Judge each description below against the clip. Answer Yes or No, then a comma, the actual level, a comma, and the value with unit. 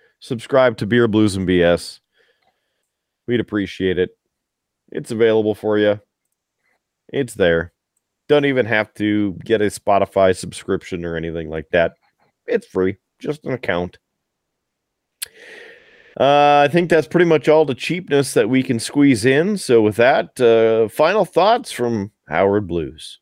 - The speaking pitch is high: No, low, 115 Hz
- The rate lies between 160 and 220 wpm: No, average, 140 wpm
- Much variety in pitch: Yes, wide, 6.8 semitones